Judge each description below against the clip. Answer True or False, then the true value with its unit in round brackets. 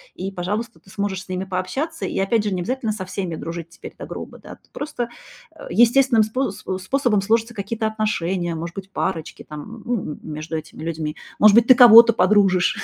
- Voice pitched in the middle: False (200 Hz)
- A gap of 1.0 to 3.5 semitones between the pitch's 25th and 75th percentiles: False (4.2 semitones)